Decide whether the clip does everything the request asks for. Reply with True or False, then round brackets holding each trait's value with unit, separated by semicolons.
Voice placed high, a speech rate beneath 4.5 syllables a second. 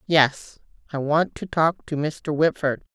False (150 Hz; 3.8 syllables/s)